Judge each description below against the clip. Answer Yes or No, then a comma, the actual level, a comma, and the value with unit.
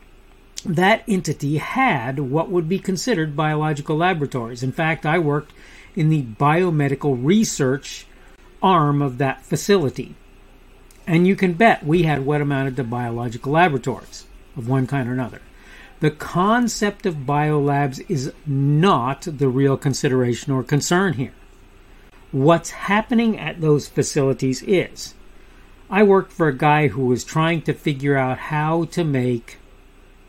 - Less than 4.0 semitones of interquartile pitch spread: No, average, 4.7 semitones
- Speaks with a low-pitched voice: No, medium, 150 Hz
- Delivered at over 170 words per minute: No, slow, 135 wpm